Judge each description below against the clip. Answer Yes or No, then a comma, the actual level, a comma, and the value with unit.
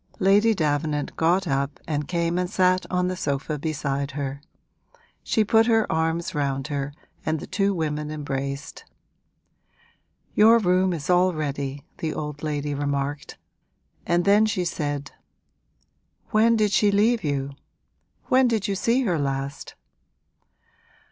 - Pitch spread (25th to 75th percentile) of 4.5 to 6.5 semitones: Yes, average, 5.3 semitones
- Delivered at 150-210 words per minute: No, slow, 135 wpm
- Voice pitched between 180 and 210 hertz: No, medium, 160 Hz